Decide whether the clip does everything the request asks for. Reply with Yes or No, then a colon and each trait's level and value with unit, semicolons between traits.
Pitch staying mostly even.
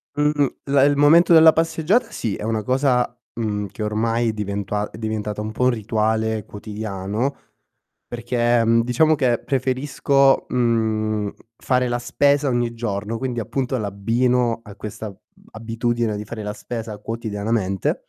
No: average, 3.2 semitones